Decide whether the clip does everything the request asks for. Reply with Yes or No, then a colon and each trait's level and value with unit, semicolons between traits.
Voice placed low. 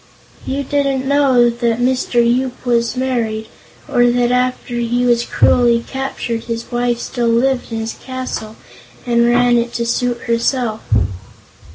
No: high, 240 Hz